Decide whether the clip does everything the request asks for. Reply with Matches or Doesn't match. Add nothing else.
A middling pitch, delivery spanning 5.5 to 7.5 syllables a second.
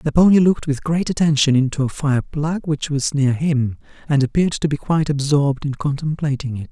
Matches